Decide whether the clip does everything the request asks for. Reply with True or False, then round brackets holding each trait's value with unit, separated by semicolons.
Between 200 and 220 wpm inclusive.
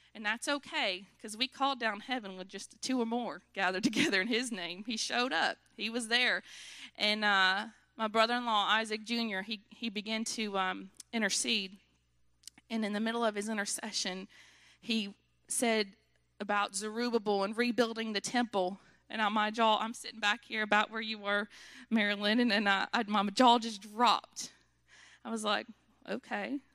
False (170 wpm)